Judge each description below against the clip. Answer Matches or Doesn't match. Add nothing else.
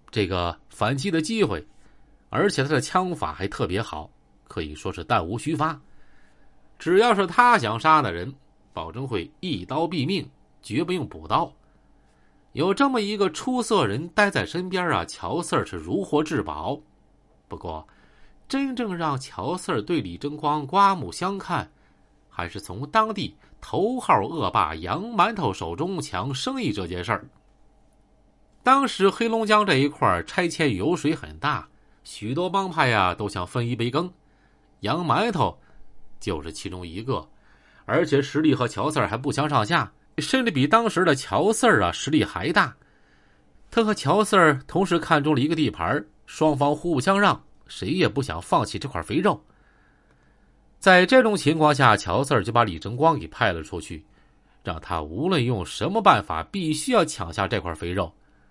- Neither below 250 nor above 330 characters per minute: Doesn't match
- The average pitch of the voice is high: Doesn't match